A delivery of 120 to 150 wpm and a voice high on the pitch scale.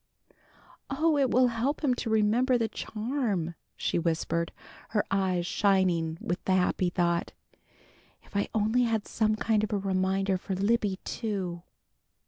Yes: average, 145 wpm; high, 205 Hz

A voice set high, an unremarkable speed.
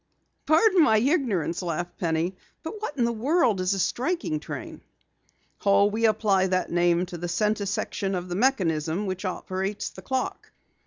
Yes: high, 200 Hz; average, 165 wpm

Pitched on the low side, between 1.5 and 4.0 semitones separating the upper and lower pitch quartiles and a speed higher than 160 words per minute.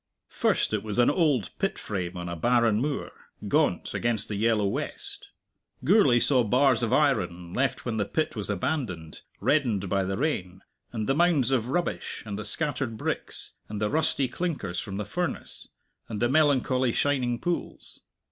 No: low, 120 Hz; wide, 5.4 semitones; average, 170 wpm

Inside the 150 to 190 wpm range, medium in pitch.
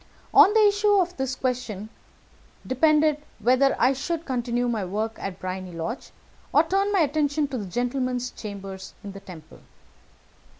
No: average, 155 wpm; very high, 250 Hz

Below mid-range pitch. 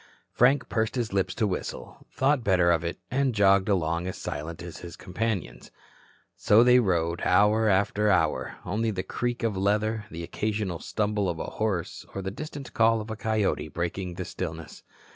Yes: low, 100 Hz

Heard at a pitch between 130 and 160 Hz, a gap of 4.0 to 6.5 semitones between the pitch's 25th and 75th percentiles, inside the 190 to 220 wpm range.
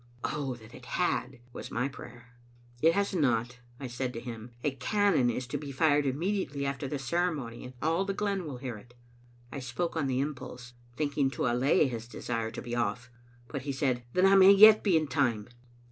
Yes: low, 135 Hz; average, 4.3 semitones; fast, 205 wpm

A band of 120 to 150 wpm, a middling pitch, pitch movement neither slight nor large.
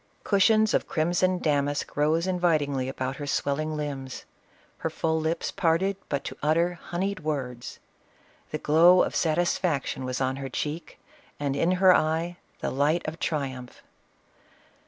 Yes: average, 140 wpm; medium, 155 Hz; average, 3.8 semitones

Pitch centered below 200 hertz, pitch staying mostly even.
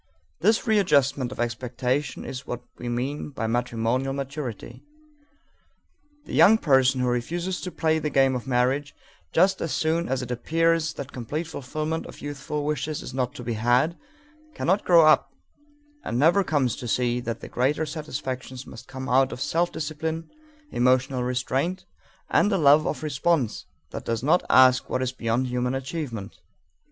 No: low, 135 Hz; average, 3.9 semitones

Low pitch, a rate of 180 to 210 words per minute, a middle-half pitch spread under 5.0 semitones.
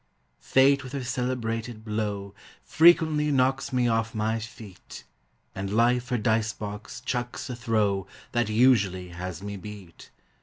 No: low, 115 Hz; average, 140 wpm; average, 3.4 semitones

